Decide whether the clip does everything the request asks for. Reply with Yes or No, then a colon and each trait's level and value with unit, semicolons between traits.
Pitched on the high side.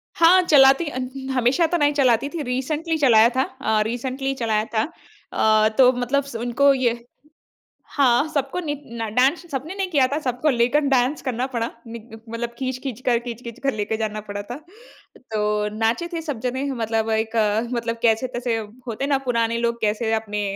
Yes: high, 245 Hz